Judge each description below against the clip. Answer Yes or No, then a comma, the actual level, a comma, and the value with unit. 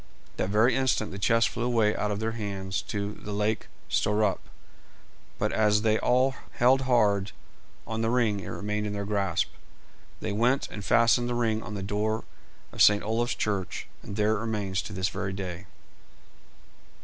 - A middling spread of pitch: No, narrow, 2.1 semitones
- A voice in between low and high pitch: No, low, 105 Hz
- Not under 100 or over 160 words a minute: No, average, 175 wpm